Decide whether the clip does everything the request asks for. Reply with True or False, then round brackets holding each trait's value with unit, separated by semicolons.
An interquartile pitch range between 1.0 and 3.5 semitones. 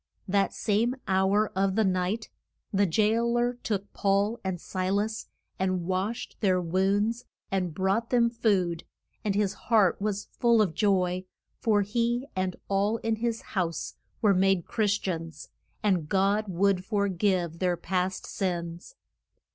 True (2.8 semitones)